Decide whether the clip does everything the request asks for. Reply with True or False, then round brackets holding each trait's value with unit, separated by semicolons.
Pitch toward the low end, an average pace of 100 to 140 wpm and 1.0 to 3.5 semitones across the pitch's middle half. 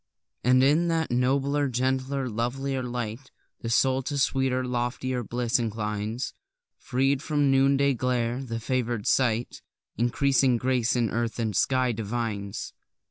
True (125 Hz; 135 wpm; 2.4 semitones)